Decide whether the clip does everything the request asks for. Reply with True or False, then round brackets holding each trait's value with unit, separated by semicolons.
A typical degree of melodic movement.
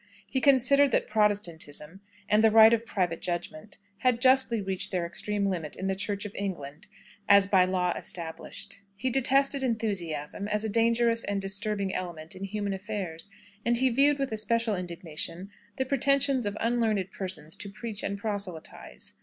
True (3.9 semitones)